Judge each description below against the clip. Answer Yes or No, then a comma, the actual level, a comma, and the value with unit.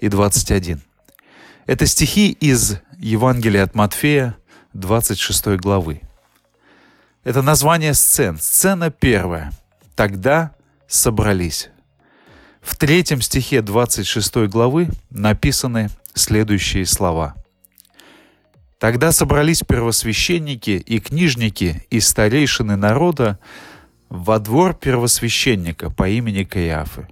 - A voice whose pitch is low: Yes, low, 110 Hz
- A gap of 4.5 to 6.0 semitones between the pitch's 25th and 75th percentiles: Yes, wide, 5.6 semitones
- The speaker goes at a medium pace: No, slow, 85 wpm